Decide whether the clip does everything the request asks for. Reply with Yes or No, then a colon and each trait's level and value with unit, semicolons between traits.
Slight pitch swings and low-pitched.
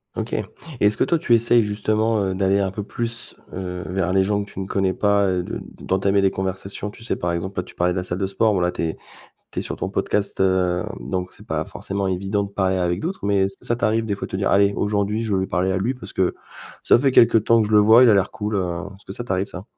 Yes: narrow, 2.2 semitones; low, 100 Hz